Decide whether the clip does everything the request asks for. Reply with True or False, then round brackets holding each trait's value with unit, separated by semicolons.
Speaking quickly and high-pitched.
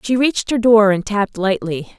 True (210 wpm; 215 Hz)